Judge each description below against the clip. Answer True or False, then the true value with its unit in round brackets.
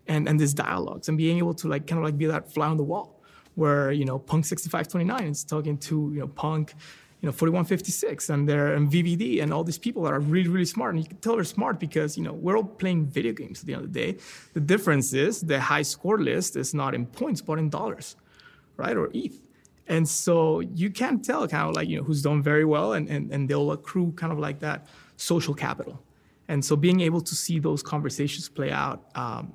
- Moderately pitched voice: True (155 Hz)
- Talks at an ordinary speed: False (240 wpm)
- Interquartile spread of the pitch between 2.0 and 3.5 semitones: True (2.7 semitones)